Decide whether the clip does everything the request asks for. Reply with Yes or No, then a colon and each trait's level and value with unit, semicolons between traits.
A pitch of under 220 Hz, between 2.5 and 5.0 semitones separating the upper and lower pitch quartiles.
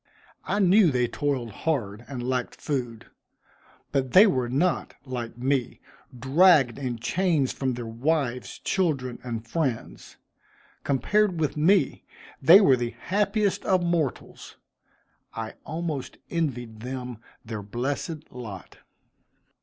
No: low, 135 Hz; wide, 5.5 semitones